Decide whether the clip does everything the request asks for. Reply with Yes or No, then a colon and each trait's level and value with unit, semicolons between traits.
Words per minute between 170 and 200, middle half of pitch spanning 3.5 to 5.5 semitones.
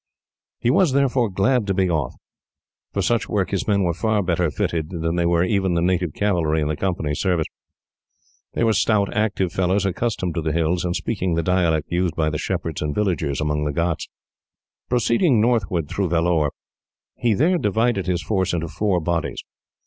Yes: average, 180 wpm; average, 4.0 semitones